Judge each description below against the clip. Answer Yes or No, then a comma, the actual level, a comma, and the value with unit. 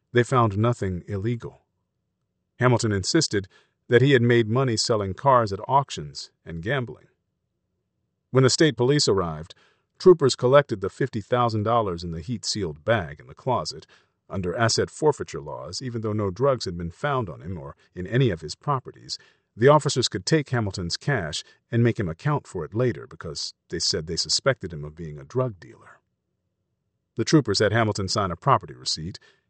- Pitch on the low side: Yes, low, 115 Hz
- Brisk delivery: Yes, fast, 175 wpm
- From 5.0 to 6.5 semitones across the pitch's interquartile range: Yes, average, 5.3 semitones